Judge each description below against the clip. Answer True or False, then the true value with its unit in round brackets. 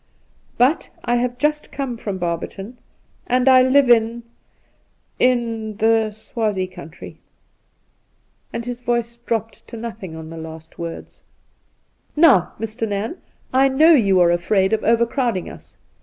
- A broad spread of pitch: False (4.0 semitones)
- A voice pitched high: True (225 Hz)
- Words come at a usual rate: True (150 wpm)